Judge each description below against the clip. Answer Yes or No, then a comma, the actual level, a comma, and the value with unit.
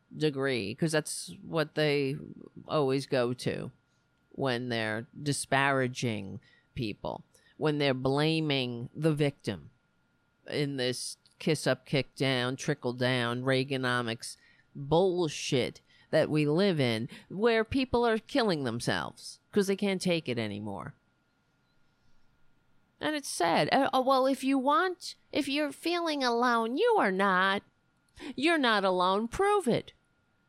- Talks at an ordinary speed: No, slow, 120 wpm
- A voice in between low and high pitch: Yes, medium, 150 Hz